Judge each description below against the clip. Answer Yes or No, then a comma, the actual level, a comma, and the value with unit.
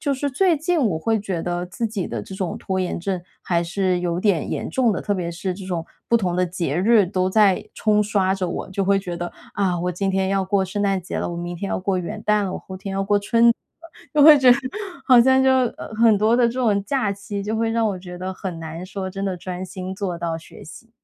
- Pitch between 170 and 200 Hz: Yes, high, 195 Hz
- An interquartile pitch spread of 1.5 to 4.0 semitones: Yes, average, 3.3 semitones